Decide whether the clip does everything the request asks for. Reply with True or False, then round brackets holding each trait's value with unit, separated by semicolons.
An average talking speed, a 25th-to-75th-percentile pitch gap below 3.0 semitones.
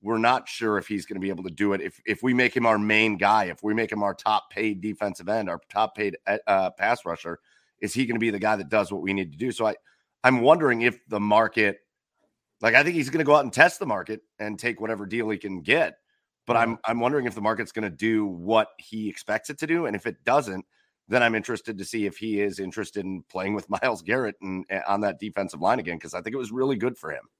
False (275 wpm; 2.4 semitones)